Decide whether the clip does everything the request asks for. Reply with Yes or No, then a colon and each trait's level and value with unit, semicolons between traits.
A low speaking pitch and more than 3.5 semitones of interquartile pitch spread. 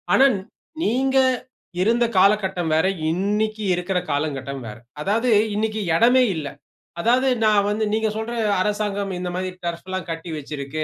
No: high, 200 Hz; average, 4.7 semitones